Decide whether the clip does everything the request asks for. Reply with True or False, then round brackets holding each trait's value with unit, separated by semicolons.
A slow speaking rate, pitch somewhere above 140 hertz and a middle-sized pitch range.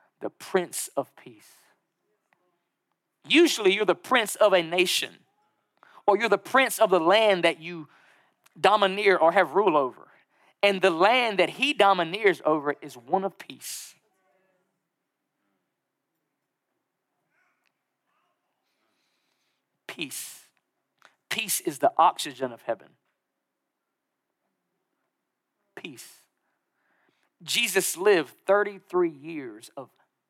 True (100 wpm; 190 Hz; 4.0 semitones)